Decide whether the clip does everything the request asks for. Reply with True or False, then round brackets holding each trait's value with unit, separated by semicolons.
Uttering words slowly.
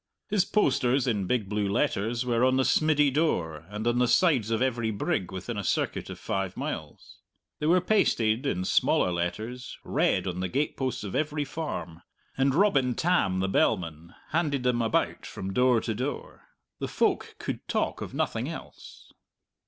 False (170 wpm)